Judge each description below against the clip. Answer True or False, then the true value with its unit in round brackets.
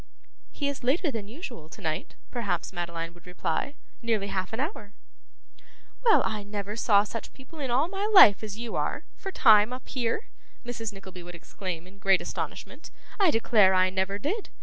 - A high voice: True (215 Hz)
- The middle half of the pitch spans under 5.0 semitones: False (5.4 semitones)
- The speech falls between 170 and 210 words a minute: True (180 wpm)